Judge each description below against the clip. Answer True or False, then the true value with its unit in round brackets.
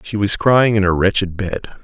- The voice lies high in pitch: False (100 Hz)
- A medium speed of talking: False (230 wpm)